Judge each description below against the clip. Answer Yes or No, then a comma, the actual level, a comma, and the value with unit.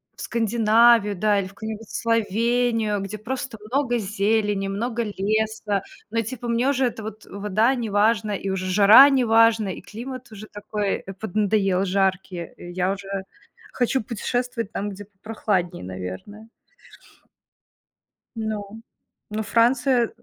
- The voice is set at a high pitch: Yes, high, 215 Hz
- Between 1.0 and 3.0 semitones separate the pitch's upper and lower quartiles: Yes, average, 2.7 semitones